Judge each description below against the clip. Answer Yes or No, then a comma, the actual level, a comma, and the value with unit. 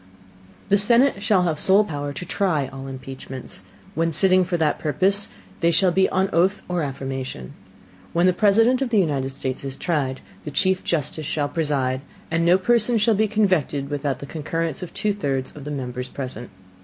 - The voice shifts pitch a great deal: Yes, wide, 5.8 semitones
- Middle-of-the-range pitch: Yes, medium, 165 Hz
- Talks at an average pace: Yes, average, 190 wpm